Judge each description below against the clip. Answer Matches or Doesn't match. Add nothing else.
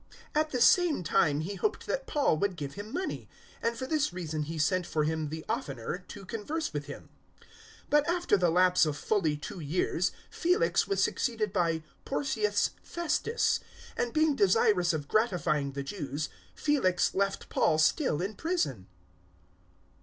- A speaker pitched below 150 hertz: Doesn't match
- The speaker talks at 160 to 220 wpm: Matches